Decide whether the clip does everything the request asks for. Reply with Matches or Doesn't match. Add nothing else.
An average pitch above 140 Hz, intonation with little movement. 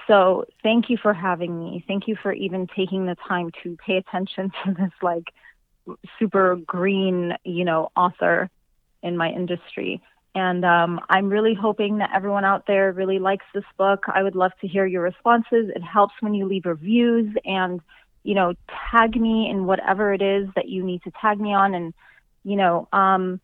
Matches